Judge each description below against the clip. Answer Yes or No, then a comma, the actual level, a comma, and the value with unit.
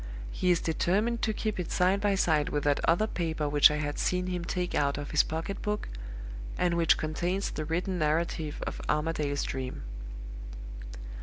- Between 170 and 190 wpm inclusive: Yes, average, 175 wpm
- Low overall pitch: No, medium, 165 Hz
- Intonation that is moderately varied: Yes, average, 3.4 semitones